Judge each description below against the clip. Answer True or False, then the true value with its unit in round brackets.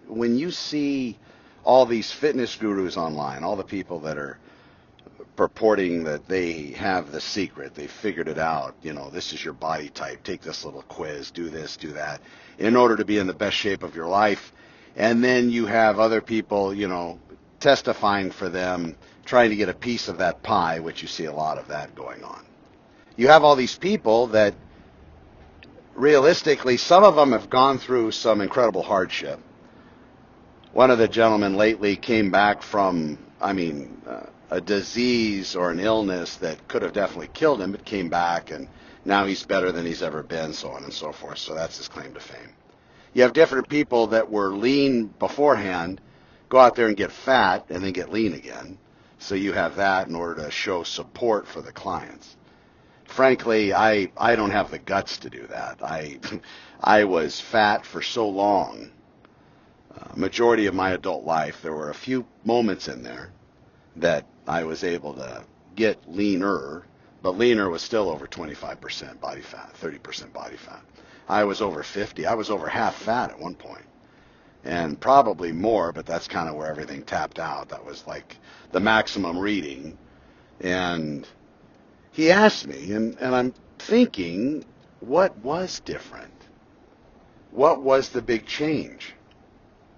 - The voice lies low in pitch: True (105 Hz)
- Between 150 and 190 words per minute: True (175 wpm)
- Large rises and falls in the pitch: True (5.9 semitones)